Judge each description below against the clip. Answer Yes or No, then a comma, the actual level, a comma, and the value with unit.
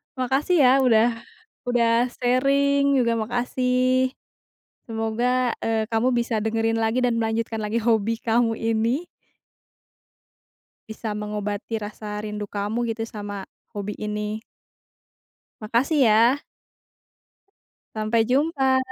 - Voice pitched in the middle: No, high, 230 Hz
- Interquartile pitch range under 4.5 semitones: Yes, narrow, 2.6 semitones